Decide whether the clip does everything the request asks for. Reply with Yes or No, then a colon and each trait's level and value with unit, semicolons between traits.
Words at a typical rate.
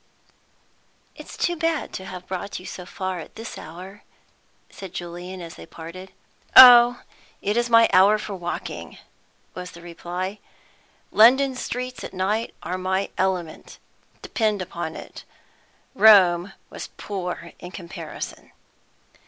No: slow, 130 wpm